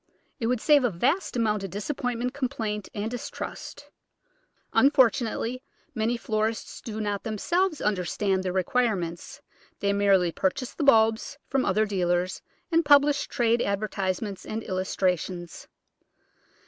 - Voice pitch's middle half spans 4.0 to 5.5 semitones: Yes, average, 4.4 semitones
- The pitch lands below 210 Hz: No, high, 220 Hz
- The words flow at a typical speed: No, slow, 125 wpm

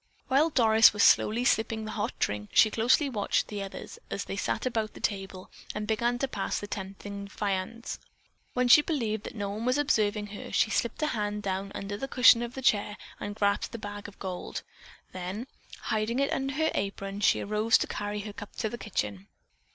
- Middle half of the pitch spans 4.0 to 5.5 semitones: No, average, 2.8 semitones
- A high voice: Yes, high, 210 Hz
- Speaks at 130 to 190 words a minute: No, fast, 205 wpm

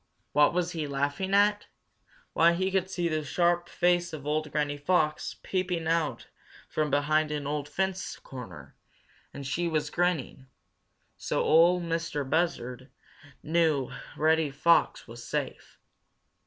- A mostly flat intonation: No, average, 3.2 semitones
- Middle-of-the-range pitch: Yes, medium, 155 Hz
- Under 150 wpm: Yes, slow, 135 wpm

